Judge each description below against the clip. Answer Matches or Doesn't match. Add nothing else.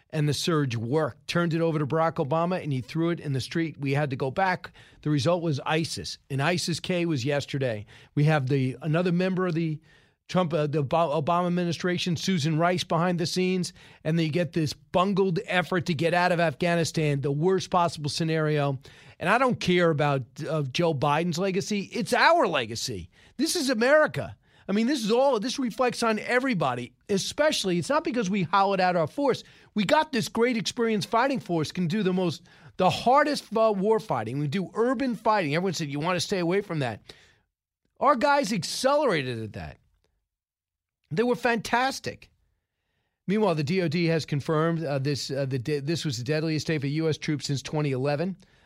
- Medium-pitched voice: Matches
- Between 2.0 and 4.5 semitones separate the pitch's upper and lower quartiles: Doesn't match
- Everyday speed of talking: Matches